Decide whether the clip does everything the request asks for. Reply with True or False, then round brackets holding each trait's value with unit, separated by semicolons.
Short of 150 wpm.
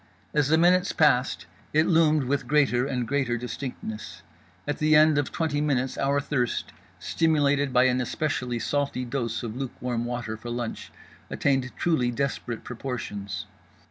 True (140 wpm)